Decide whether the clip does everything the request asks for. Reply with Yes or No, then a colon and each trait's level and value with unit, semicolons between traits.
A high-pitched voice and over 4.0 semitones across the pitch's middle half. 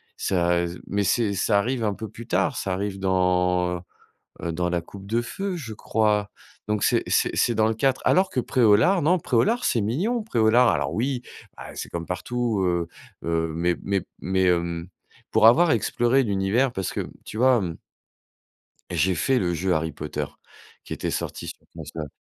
No: low, 105 Hz; average, 5.3 semitones